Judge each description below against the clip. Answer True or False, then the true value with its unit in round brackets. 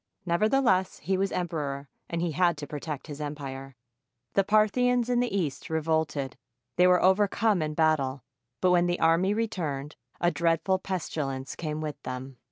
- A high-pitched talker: False (165 Hz)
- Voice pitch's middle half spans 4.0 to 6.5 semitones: True (4.5 semitones)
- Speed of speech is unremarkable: True (165 wpm)